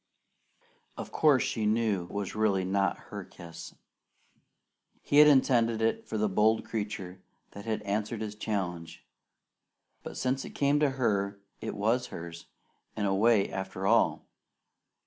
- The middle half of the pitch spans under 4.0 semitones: Yes, average, 3.0 semitones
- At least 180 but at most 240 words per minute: No, average, 145 wpm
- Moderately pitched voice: No, low, 105 Hz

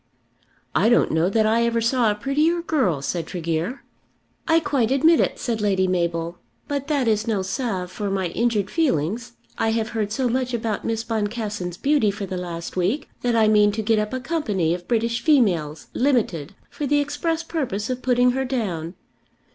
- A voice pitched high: Yes, high, 225 Hz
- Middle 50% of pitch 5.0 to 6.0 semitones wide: Yes, average, 5.3 semitones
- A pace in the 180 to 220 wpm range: Yes, average, 185 wpm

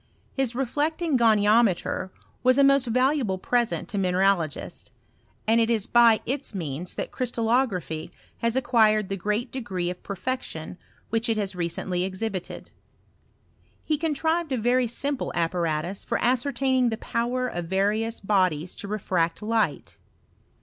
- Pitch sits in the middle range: No, high, 220 Hz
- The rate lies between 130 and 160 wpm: Yes, average, 140 wpm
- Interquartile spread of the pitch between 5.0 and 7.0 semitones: Yes, average, 5.3 semitones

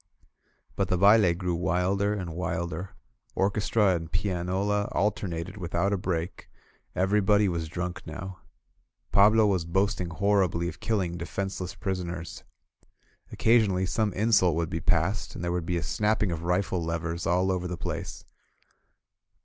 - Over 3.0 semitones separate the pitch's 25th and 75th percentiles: No, narrow, 2.6 semitones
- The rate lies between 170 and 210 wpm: No, average, 140 wpm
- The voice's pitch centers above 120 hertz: No, very low, 90 Hz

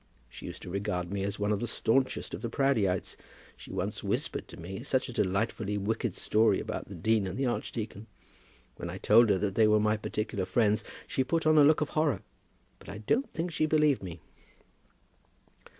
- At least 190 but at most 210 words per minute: Yes, average, 200 wpm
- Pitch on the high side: No, low, 110 Hz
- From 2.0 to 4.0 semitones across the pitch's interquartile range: No, average, 4.8 semitones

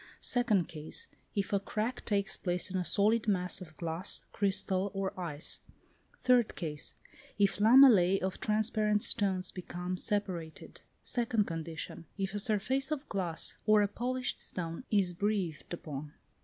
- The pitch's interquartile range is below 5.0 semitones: Yes, average, 3.3 semitones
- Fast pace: No, average, 140 wpm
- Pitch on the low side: No, high, 195 Hz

